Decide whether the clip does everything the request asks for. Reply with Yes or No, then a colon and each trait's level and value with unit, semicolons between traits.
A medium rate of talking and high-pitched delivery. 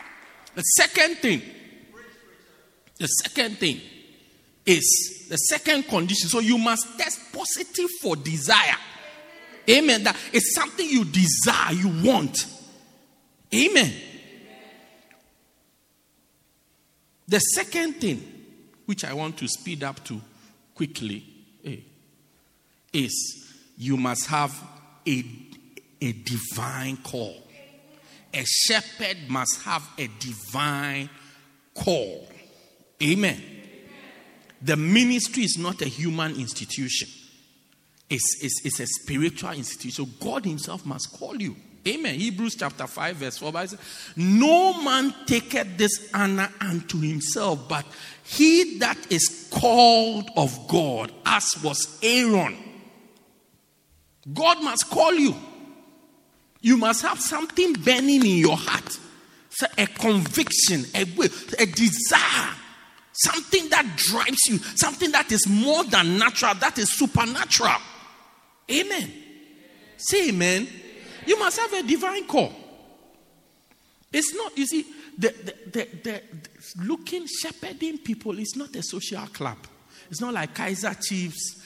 No: slow, 115 wpm; high, 210 Hz